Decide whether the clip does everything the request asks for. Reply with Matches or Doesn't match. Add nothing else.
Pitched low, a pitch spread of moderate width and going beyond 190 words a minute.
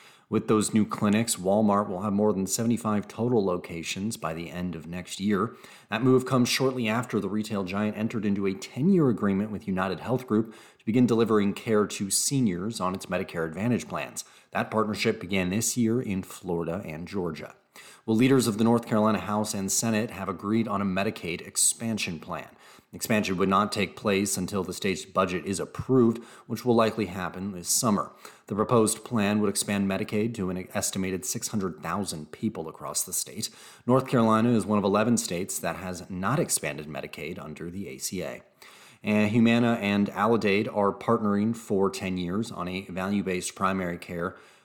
Doesn't match